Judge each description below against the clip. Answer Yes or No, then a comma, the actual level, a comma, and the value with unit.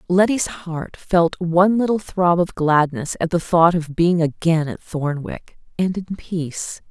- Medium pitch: Yes, medium, 170 Hz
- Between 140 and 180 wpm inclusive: Yes, average, 165 wpm